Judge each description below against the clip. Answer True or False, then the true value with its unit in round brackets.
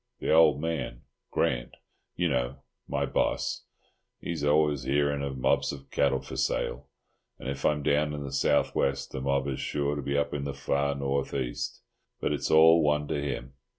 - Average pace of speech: True (175 wpm)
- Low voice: True (70 Hz)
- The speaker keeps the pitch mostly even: True (1.5 semitones)